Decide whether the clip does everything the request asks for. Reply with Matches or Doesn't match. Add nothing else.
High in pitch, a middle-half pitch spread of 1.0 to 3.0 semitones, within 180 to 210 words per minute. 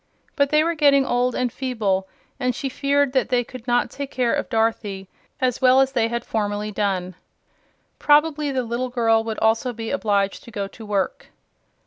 Doesn't match